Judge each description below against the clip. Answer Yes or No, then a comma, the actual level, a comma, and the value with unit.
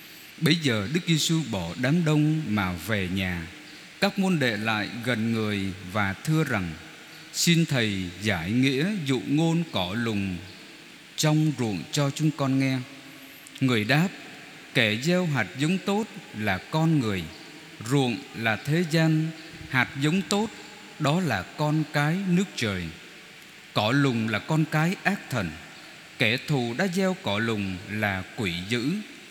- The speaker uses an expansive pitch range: Yes, wide, 6.9 semitones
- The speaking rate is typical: No, slow, 145 wpm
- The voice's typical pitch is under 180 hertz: Yes, medium, 140 Hz